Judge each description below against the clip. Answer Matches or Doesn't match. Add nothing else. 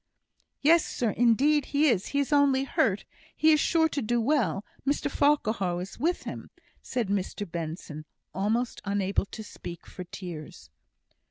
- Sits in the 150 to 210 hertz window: Doesn't match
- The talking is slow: Doesn't match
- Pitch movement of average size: Doesn't match